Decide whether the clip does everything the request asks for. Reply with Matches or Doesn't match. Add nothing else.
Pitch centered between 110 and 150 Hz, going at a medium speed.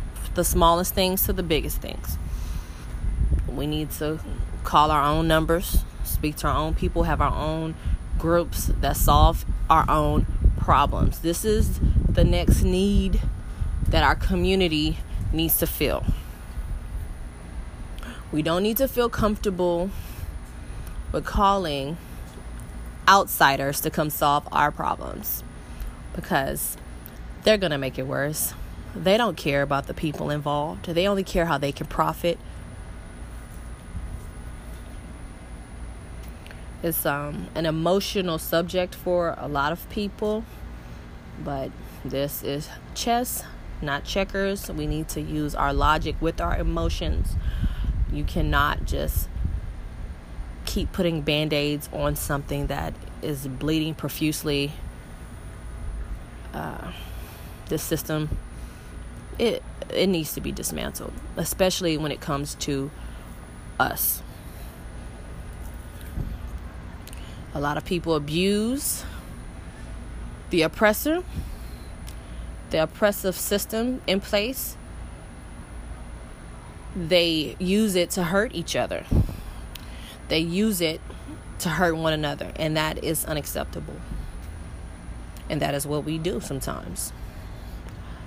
Doesn't match